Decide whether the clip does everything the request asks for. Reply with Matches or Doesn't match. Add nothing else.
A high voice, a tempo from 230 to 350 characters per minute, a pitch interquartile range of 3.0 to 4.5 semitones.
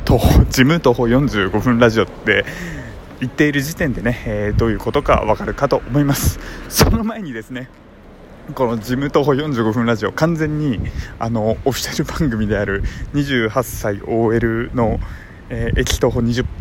Doesn't match